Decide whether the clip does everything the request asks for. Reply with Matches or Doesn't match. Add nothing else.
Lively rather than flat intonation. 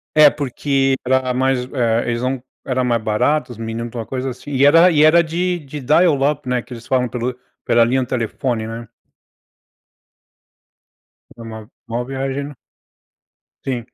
Doesn't match